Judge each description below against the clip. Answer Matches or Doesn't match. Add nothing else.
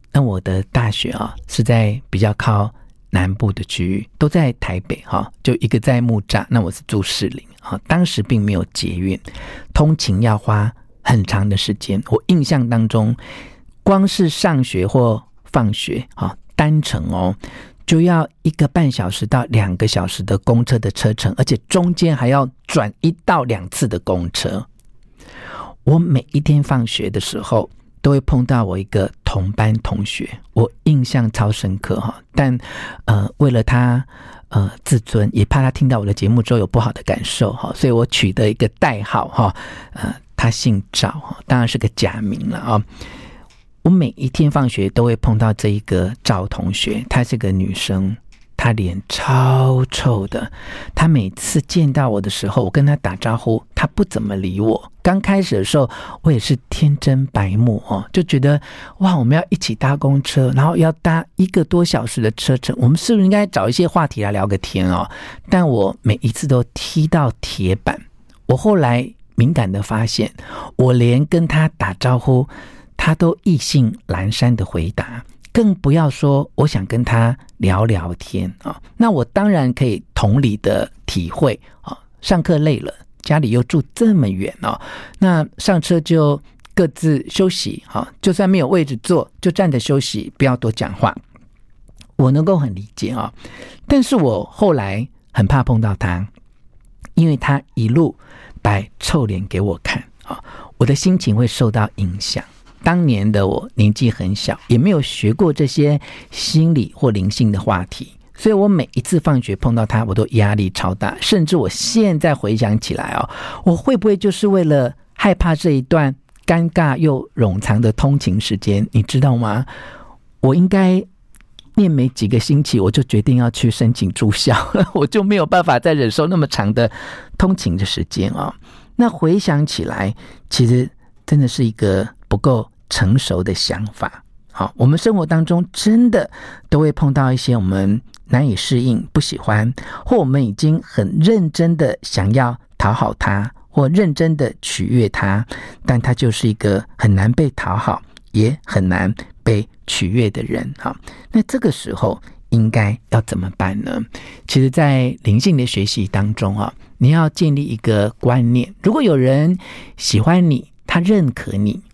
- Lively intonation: Matches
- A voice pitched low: Matches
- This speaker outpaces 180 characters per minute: Matches